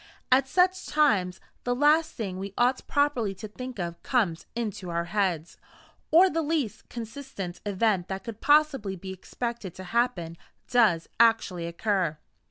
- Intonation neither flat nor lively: No, wide, 5.8 semitones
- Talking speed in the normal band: Yes, average, 150 wpm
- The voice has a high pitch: Yes, high, 215 Hz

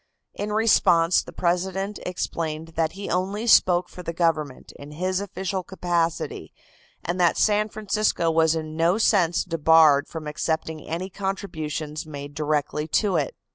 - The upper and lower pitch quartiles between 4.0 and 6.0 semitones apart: No, average, 3.3 semitones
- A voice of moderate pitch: Yes, medium, 170 Hz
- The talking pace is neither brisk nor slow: Yes, average, 145 wpm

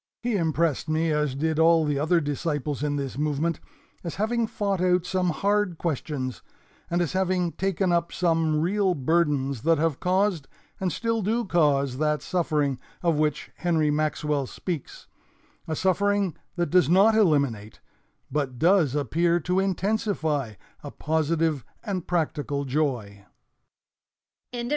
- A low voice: No, medium, 160 Hz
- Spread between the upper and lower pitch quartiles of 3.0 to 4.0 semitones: Yes, average, 3.7 semitones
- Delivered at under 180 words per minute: Yes, average, 140 wpm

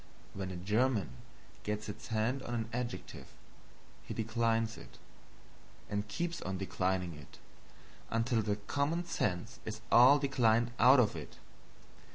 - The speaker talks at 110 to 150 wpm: Yes, slow, 135 wpm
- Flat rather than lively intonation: No, average, 3.6 semitones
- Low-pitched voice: Yes, low, 110 Hz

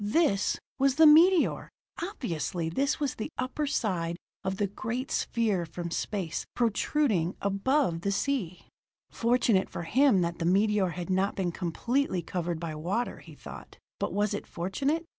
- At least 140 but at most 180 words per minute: Yes, average, 155 wpm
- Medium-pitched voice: No, high, 200 Hz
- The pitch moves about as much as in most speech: No, wide, 6.9 semitones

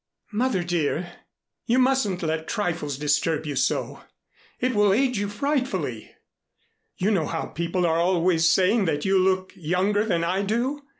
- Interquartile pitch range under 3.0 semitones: No, average, 4.2 semitones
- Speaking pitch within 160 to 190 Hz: Yes, medium, 185 Hz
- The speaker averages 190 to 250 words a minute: No, average, 155 wpm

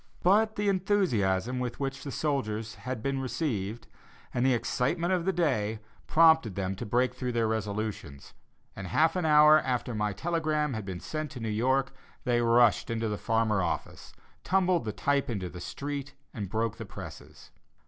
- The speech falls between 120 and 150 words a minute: No, average, 175 wpm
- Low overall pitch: Yes, low, 125 Hz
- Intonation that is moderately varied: No, wide, 5.9 semitones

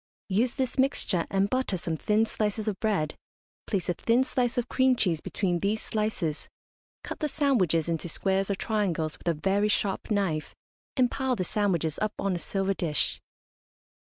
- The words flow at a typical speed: Yes, average, 175 wpm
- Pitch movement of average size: Yes, average, 4.7 semitones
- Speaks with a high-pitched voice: Yes, high, 200 Hz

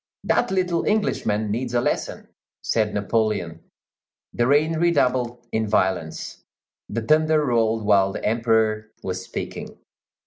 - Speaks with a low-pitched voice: Yes, low, 115 Hz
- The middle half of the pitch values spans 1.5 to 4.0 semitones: No, average, 4.8 semitones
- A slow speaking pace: Yes, slow, 125 wpm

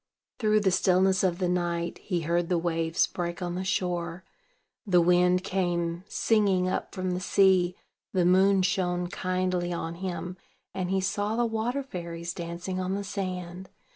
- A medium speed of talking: Yes, average, 165 wpm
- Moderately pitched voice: Yes, medium, 180 Hz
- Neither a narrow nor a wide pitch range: No, narrow, 1.6 semitones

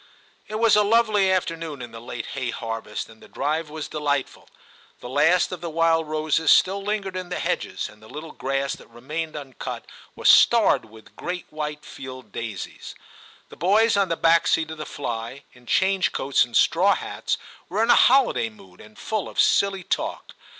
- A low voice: No, medium, 155 Hz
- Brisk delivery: No, average, 190 wpm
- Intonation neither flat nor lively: No, wide, 6.3 semitones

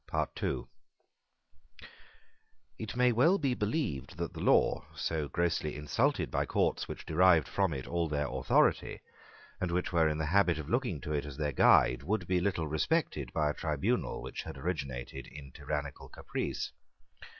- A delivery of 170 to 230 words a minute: No, average, 160 wpm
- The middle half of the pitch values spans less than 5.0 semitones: Yes, average, 4.4 semitones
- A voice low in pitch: Yes, very low, 80 Hz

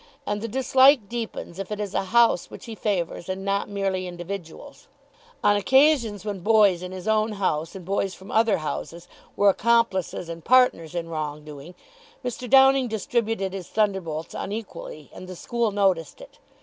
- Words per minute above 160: Yes, average, 170 wpm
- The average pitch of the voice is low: No, high, 200 Hz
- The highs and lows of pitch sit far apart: No, average, 4.2 semitones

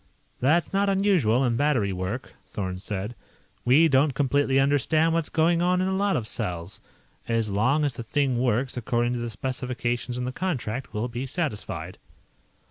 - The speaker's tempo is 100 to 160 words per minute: No, average, 170 wpm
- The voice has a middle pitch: No, low, 130 Hz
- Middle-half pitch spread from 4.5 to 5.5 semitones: Yes, average, 4.9 semitones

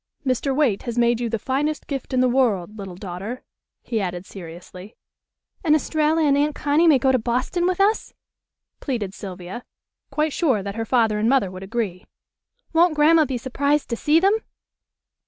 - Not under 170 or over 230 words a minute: Yes, average, 175 wpm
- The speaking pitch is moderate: No, very high, 250 Hz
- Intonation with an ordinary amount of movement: No, wide, 6.3 semitones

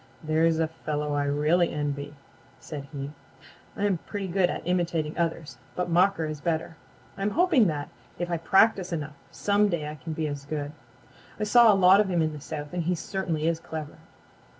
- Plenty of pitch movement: No, average, 3.3 semitones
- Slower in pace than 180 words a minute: No, average, 190 wpm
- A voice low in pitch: No, medium, 165 Hz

